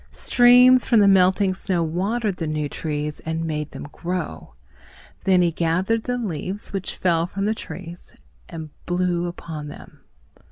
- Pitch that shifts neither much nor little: Yes, average, 3.5 semitones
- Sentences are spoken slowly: No, average, 155 wpm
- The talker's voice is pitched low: No, medium, 180 Hz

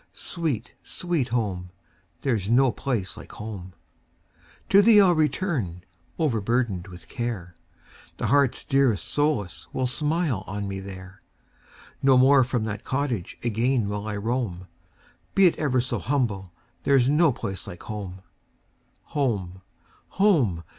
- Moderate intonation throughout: No, wide, 6.2 semitones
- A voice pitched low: Yes, low, 120 Hz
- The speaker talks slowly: Yes, slow, 120 wpm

